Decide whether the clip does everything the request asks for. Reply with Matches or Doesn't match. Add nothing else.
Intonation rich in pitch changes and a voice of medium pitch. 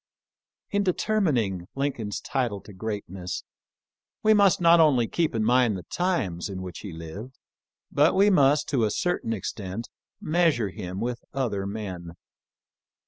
Doesn't match